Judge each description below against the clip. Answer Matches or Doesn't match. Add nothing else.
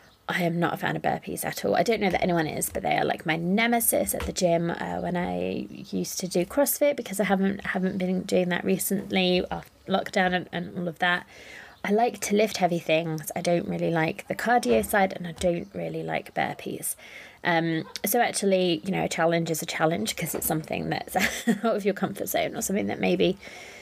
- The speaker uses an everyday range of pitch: Matches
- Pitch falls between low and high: Matches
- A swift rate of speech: Matches